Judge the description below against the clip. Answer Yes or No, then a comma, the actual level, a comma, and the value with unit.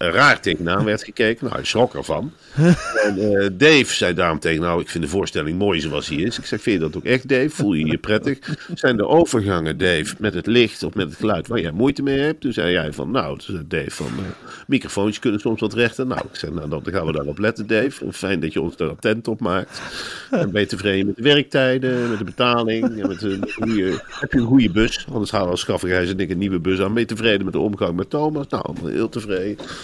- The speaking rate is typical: No, fast, 245 wpm